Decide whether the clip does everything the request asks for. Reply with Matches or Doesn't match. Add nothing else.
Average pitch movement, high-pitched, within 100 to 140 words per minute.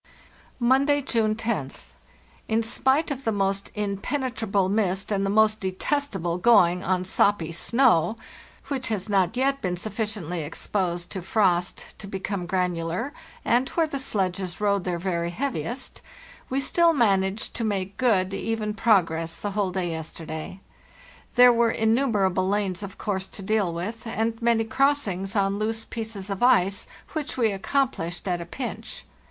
Doesn't match